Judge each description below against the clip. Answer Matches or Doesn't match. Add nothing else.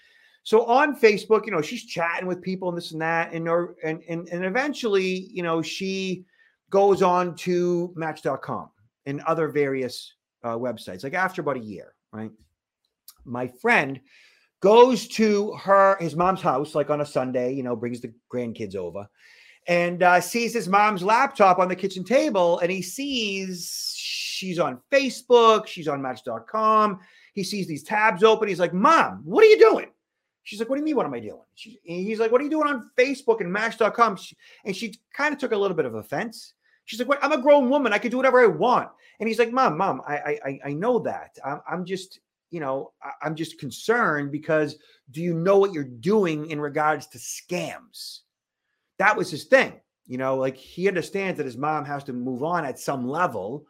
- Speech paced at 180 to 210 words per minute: Matches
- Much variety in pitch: Matches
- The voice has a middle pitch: Matches